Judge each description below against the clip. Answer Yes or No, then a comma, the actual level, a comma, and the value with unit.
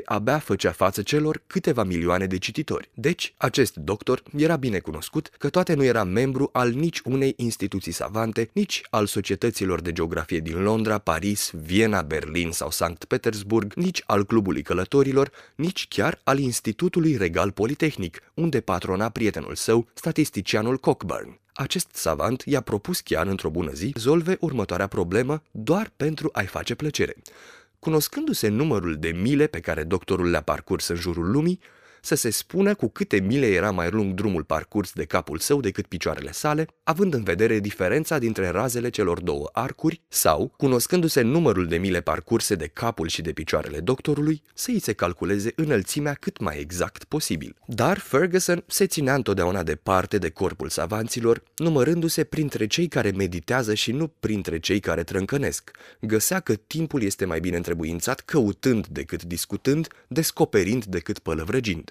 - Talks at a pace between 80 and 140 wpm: No, average, 155 wpm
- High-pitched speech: No, low, 115 Hz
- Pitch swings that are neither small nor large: No, wide, 7.9 semitones